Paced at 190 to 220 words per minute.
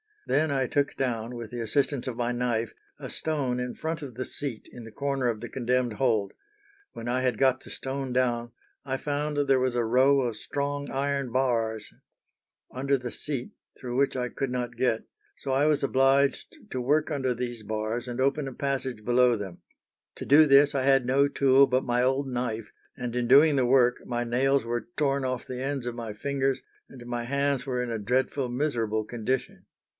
Yes: average, 200 wpm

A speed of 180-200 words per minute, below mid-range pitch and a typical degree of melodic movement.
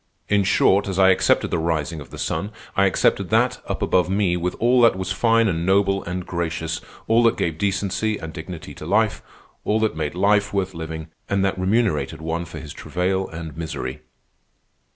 Yes: average, 195 wpm; very low, 95 Hz; average, 3.4 semitones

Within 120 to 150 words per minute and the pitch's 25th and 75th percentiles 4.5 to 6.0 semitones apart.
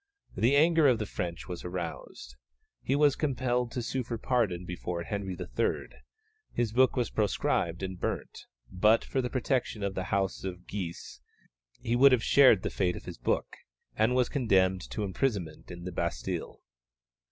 No: average, 170 wpm; wide, 5.6 semitones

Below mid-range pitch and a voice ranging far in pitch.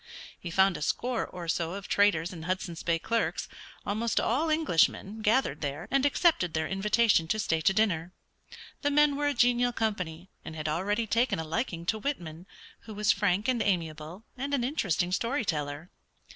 No: high, 200 Hz; wide, 6.0 semitones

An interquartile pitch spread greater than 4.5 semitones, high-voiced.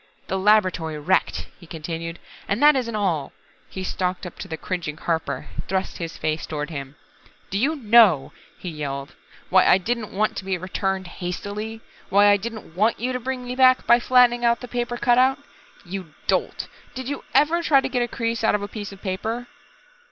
Yes: average, 5.3 semitones; high, 200 Hz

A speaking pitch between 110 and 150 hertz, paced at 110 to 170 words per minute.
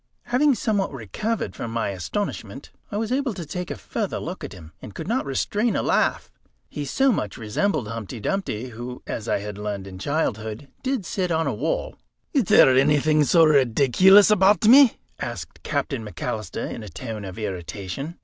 No: medium, 140 Hz; average, 180 wpm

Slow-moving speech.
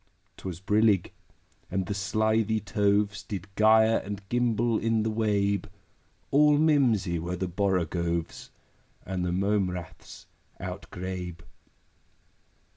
Yes: slow, 110 wpm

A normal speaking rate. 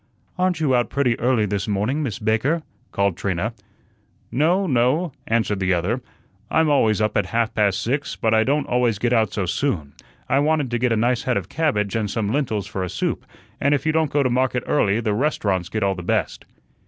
No: fast, 215 wpm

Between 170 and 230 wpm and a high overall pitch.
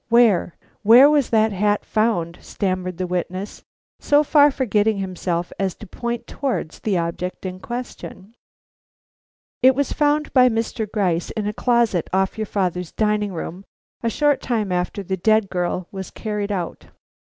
No: average, 155 wpm; high, 210 Hz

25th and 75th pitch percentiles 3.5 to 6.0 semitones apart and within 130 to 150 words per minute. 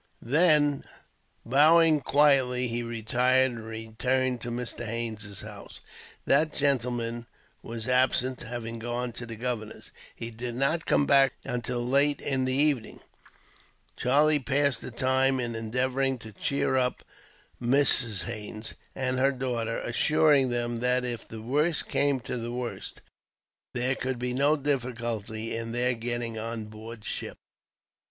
No: narrow, 2.6 semitones; average, 140 wpm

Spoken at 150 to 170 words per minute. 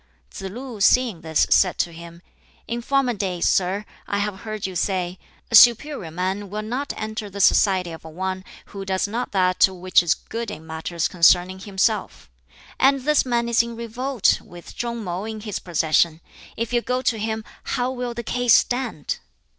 No: average, 180 wpm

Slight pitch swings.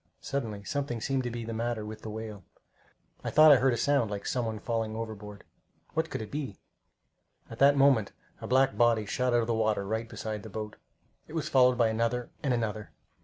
No: average, 3.0 semitones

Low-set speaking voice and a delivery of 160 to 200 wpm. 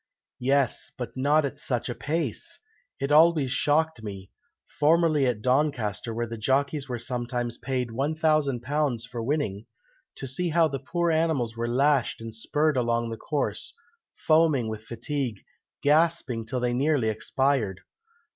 No: low, 130 Hz; average, 145 wpm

